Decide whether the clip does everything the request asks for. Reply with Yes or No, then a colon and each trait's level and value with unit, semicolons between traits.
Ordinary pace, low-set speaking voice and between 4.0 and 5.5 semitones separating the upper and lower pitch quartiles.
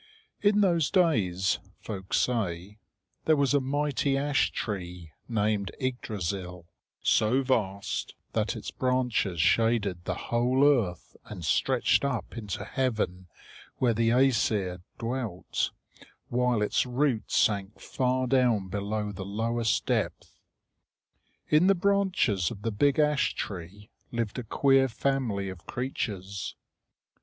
No: slow, 120 wpm; low, 115 Hz; average, 5.0 semitones